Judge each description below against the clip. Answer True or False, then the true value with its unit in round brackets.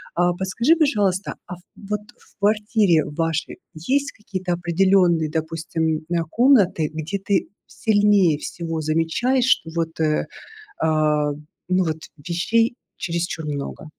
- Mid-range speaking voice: True (175 Hz)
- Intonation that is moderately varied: True (4.3 semitones)